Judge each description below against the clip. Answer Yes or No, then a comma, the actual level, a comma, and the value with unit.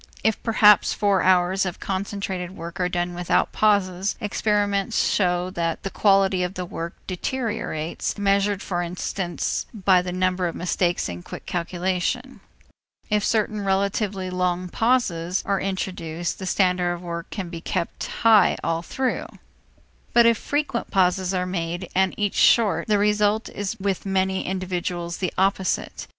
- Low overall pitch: No, high, 190 Hz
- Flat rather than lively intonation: Yes, narrow, 2.3 semitones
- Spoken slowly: No, average, 150 wpm